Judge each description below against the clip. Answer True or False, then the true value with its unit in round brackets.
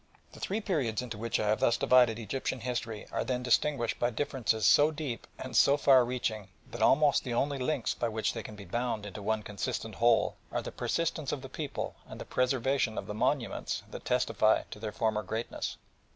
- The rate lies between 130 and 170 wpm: False (205 wpm)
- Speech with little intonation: False (3.4 semitones)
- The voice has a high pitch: False (120 Hz)